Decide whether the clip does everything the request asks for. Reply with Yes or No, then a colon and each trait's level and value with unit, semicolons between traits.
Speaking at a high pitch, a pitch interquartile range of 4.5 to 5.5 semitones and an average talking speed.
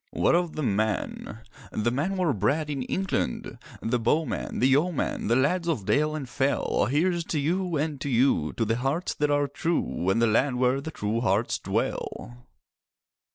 No: medium, 140 Hz; average, 5.2 semitones; average, 170 wpm